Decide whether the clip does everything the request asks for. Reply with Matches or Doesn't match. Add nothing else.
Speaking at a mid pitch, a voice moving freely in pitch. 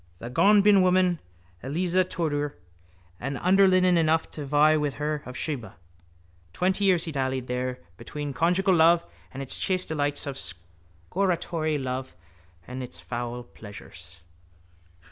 Matches